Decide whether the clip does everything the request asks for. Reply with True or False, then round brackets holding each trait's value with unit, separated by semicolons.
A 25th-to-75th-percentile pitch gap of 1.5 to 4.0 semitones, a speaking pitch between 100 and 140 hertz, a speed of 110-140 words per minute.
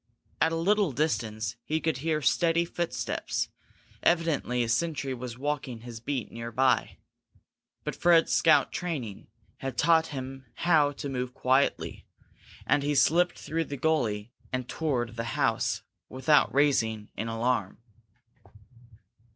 False (5.2 semitones; 135 Hz; 135 wpm)